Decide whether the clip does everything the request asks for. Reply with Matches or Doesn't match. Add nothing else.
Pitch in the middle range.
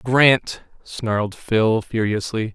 Doesn't match